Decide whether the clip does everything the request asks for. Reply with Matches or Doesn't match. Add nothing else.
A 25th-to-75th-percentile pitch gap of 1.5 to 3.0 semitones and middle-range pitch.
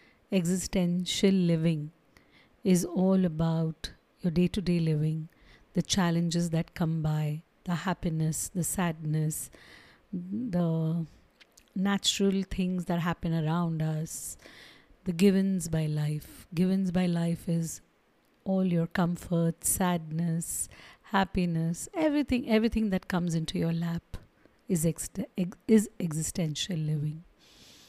Matches